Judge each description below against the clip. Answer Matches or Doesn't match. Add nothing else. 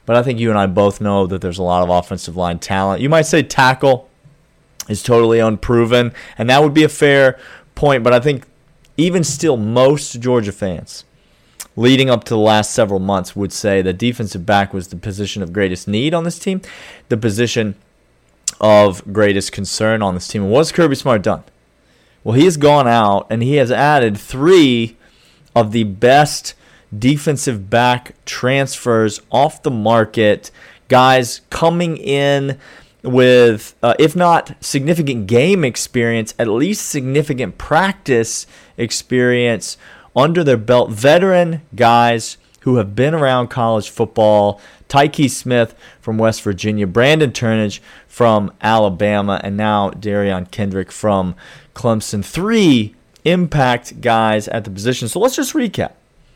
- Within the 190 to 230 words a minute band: Doesn't match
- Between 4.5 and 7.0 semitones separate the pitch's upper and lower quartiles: Matches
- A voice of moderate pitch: Doesn't match